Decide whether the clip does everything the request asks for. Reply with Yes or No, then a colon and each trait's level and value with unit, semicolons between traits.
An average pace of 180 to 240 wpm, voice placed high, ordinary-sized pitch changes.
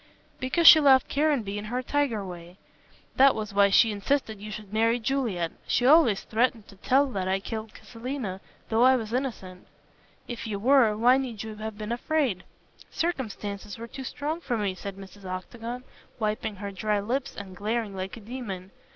Yes: average, 185 wpm; high, 220 Hz; average, 4.2 semitones